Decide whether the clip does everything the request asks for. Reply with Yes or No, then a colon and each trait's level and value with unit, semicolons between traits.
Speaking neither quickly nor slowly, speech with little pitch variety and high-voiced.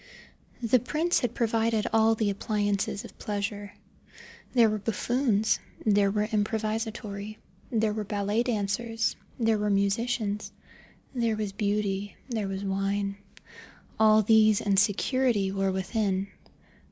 No: slow, 120 wpm; narrow, 1.9 semitones; high, 210 Hz